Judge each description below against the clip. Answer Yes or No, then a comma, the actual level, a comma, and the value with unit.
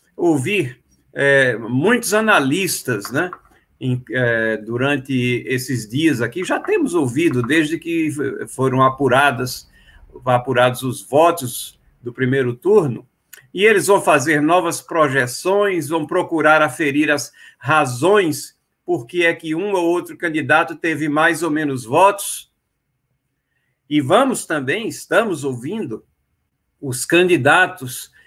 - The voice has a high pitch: No, medium, 150 Hz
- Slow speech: Yes, slow, 115 wpm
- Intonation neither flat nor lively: Yes, average, 5.0 semitones